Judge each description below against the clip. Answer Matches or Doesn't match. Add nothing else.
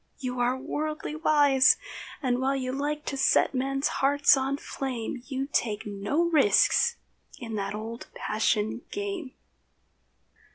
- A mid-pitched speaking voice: Doesn't match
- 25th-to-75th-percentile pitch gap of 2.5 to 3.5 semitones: Matches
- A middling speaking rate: Doesn't match